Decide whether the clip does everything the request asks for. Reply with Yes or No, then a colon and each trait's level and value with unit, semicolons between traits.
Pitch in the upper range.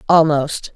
No: medium, 150 Hz